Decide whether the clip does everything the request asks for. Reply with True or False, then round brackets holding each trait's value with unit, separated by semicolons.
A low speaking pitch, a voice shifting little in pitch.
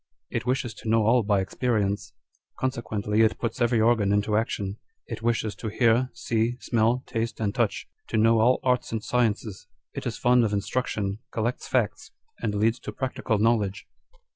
True (115 Hz; 2.3 semitones)